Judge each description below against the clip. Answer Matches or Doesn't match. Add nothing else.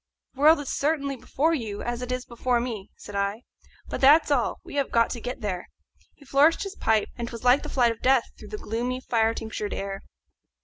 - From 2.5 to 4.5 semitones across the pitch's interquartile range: Matches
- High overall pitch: Matches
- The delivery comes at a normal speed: Doesn't match